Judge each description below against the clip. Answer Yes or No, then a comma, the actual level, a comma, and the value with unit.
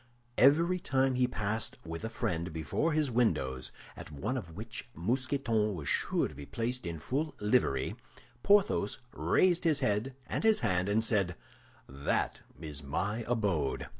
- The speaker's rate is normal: Yes, average, 155 wpm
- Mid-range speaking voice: No, low, 110 Hz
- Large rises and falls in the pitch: Yes, wide, 7.8 semitones